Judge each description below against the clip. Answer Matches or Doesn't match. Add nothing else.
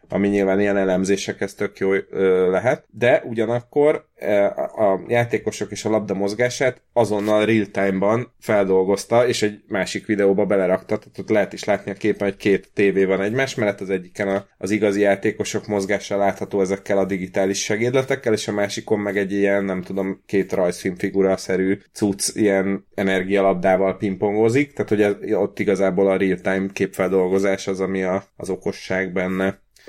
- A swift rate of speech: Doesn't match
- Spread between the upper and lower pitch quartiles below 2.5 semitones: Matches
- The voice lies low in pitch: Matches